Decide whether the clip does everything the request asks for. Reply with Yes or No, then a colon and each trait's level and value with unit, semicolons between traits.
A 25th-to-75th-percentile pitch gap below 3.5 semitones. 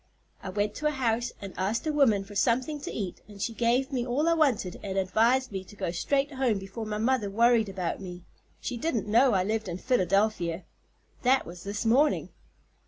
No: average, 4.8 semitones